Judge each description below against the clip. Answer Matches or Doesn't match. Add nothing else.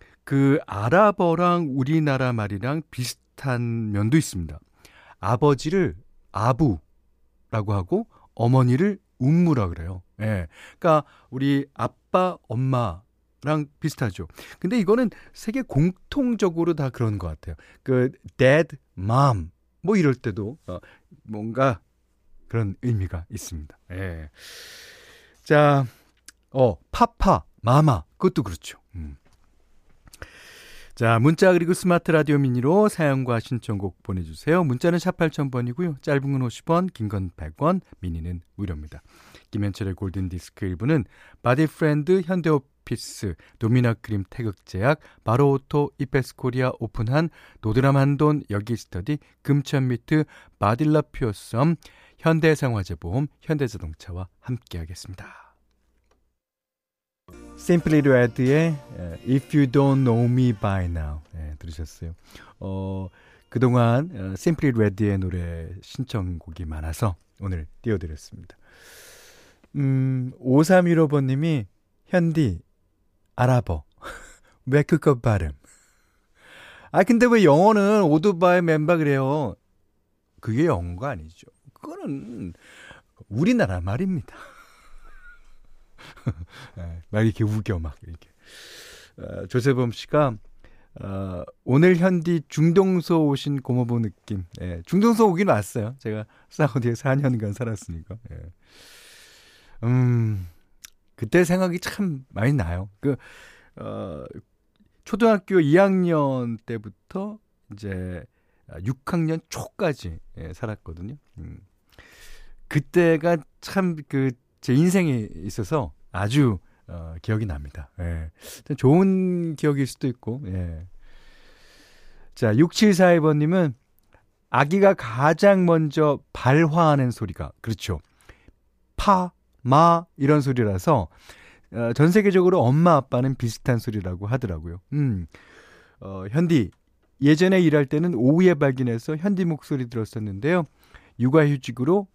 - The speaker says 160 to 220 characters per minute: Doesn't match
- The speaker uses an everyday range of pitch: Doesn't match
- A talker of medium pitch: Doesn't match